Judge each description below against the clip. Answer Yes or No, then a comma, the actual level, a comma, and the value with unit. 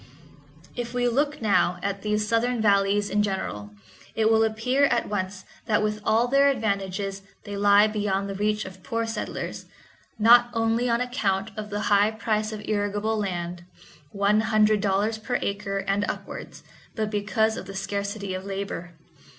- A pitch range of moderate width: No, narrow, 2.0 semitones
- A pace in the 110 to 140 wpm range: No, average, 160 wpm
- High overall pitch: Yes, high, 210 Hz